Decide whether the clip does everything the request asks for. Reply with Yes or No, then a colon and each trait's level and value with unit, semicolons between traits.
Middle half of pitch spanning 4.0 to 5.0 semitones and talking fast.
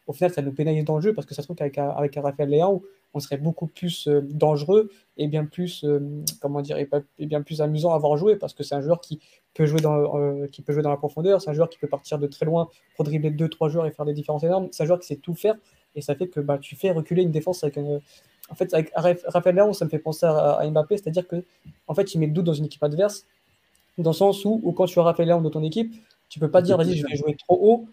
No: average, 3.3 semitones; fast, 295 wpm